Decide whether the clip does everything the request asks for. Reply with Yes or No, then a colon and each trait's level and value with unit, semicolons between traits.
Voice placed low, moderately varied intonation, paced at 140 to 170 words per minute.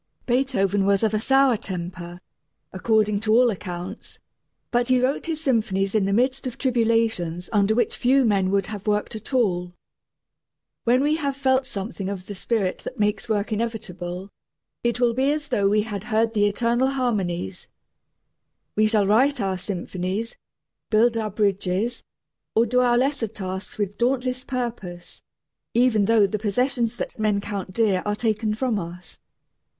No: high, 215 Hz; average, 3.7 semitones; average, 160 wpm